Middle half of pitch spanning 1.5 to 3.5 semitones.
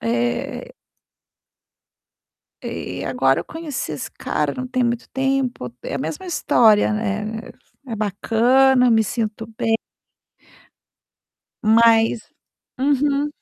No: average, 3.9 semitones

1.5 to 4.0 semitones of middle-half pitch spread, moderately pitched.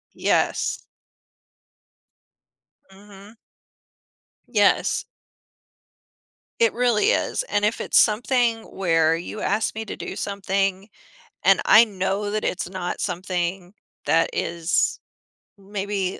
No: narrow, 2.5 semitones; high, 200 Hz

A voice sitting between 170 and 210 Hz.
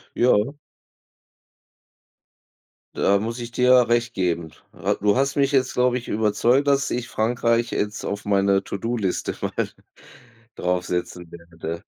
No: low, 110 Hz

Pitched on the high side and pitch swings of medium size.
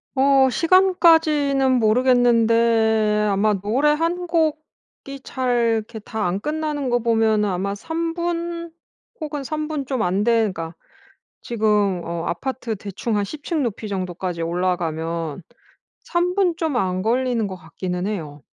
No: high, 230 Hz; wide, 7.2 semitones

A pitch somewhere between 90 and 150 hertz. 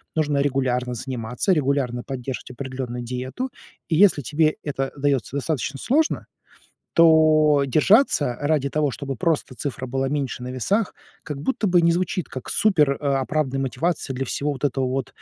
Yes: medium, 140 Hz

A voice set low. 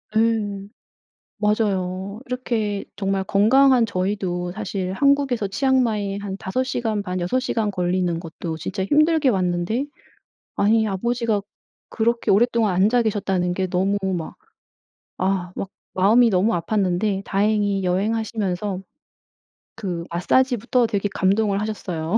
No: high, 205 Hz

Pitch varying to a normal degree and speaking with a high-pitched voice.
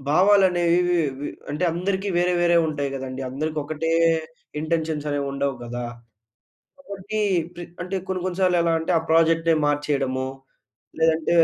No: average, 3.7 semitones; medium, 165 Hz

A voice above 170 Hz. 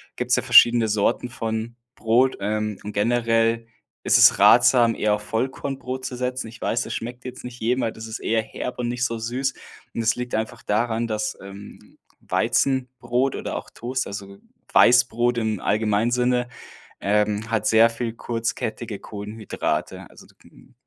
No: low, 115 Hz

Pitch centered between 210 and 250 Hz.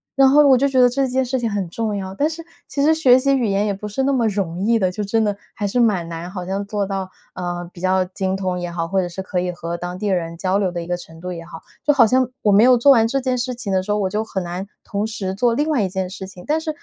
No: high, 200 Hz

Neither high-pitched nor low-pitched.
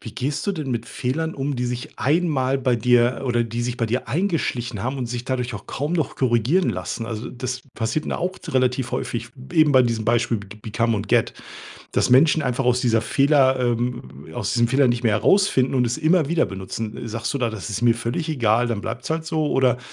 No: low, 125 Hz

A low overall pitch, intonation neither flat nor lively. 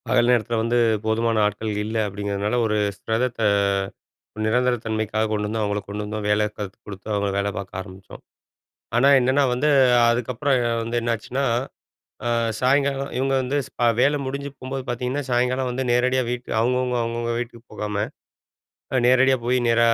Yes: low, 120 Hz; average, 3.0 semitones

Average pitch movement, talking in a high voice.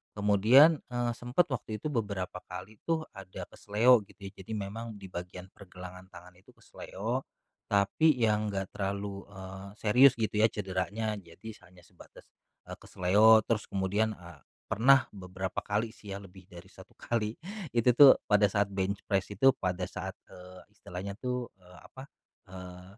No: average, 3.2 semitones; low, 100 Hz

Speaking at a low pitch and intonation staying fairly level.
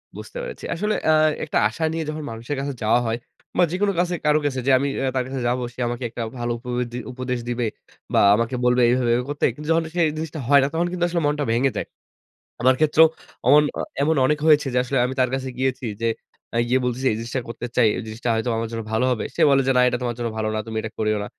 No: low, 130 Hz; average, 3.8 semitones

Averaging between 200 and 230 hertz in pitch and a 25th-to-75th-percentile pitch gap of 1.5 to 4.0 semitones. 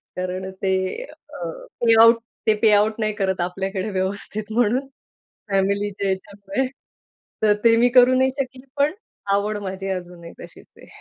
Yes: high, 205 Hz; average, 3.5 semitones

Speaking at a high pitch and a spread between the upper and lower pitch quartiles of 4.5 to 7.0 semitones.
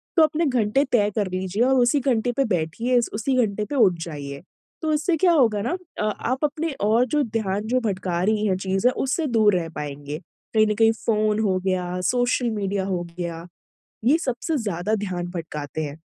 Yes: high, 215 Hz; average, 5.2 semitones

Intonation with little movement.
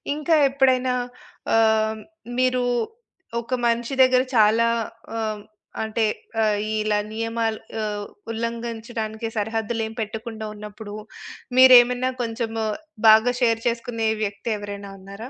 Yes: narrow, 1.8 semitones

